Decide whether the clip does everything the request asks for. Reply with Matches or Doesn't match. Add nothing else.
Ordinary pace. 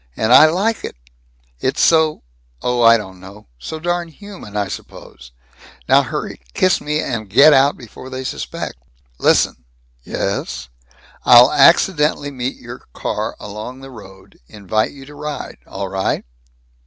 Matches